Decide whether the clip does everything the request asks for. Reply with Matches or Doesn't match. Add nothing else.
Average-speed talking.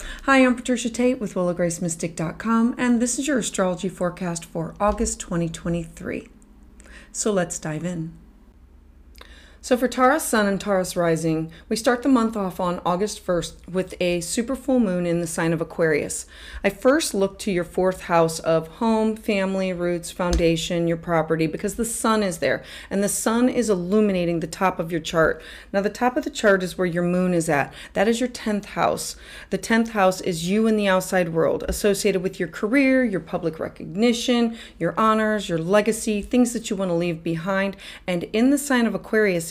Matches